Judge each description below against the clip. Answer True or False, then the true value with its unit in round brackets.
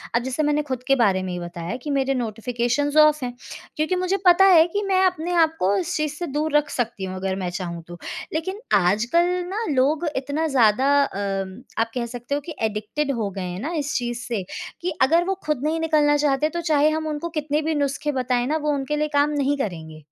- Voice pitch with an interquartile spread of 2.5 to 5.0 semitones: False (5.4 semitones)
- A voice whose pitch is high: True (280 Hz)